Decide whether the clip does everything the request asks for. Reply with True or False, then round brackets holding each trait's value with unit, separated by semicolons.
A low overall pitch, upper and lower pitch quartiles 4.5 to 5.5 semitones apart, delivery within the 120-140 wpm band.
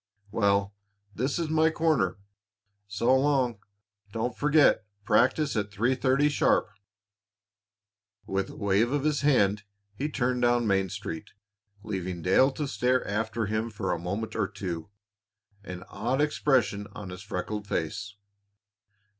True (110 Hz; 4.9 semitones; 135 wpm)